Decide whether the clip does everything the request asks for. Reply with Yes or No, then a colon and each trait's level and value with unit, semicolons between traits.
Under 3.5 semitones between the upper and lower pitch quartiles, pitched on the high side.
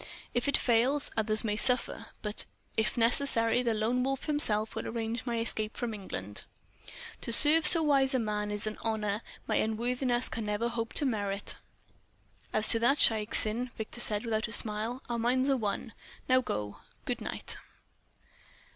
Yes: average, 2.7 semitones; high, 230 Hz